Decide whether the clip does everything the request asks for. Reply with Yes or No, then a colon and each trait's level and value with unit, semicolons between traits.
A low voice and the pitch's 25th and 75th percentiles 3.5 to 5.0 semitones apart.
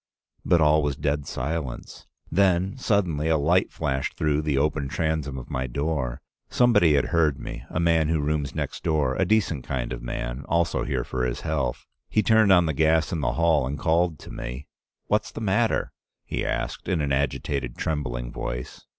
Yes: very low, 75 Hz; average, 3.8 semitones